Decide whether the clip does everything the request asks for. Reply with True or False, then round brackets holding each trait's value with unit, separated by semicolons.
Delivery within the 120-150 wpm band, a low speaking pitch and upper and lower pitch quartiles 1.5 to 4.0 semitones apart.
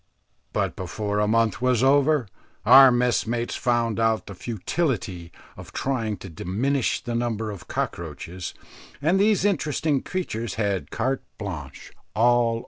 False (145 wpm; 115 Hz; 4.4 semitones)